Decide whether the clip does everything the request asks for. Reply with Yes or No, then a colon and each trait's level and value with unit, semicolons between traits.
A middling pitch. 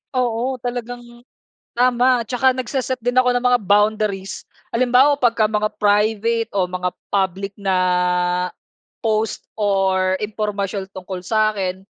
No: high, 215 Hz